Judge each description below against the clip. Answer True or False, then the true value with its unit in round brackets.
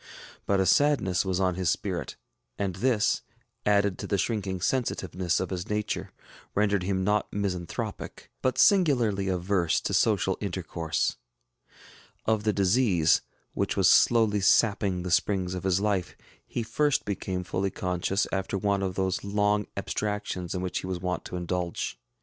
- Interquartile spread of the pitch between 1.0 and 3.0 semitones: True (2.4 semitones)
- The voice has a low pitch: True (95 Hz)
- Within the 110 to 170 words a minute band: True (155 wpm)